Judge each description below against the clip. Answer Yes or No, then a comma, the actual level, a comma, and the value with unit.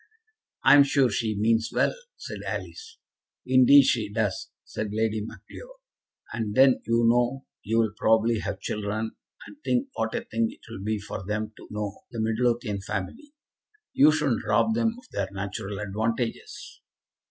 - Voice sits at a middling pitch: No, low, 115 Hz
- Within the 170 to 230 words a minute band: No, average, 155 wpm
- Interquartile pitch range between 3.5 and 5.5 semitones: Yes, average, 4.4 semitones